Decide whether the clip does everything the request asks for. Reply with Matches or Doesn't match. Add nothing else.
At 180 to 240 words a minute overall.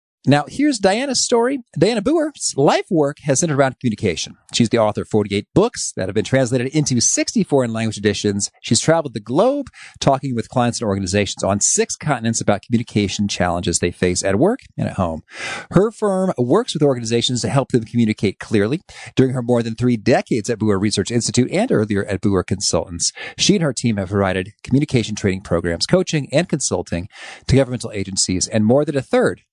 Matches